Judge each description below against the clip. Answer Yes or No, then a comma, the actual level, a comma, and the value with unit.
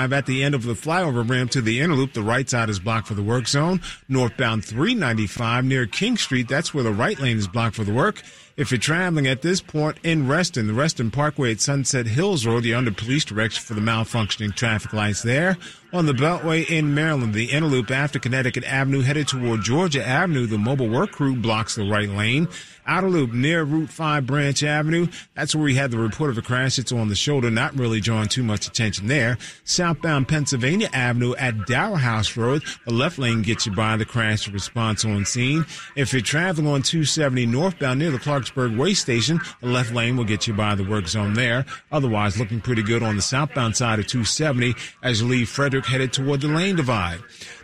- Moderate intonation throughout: Yes, average, 4.6 semitones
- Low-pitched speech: Yes, low, 125 Hz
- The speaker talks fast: Yes, fast, 210 wpm